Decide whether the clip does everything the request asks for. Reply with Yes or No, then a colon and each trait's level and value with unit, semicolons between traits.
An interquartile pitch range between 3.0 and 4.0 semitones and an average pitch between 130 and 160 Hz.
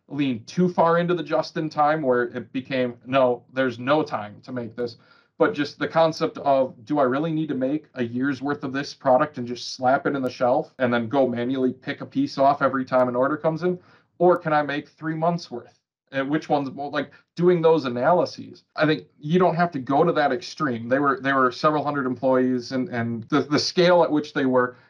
Yes: average, 3.6 semitones; medium, 140 Hz